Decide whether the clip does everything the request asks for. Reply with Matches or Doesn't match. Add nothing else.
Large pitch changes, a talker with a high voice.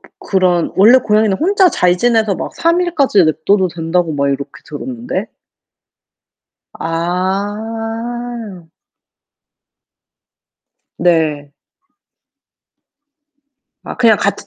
Matches